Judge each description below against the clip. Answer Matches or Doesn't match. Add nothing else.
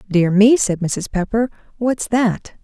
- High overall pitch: Matches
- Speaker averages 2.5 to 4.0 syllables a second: Matches